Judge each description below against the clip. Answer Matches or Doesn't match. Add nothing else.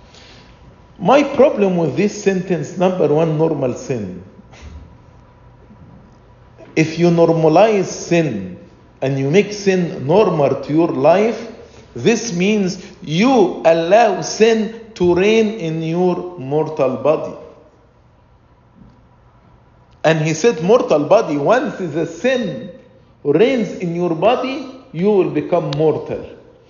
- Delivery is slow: Matches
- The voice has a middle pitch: Matches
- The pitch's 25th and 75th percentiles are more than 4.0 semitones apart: Matches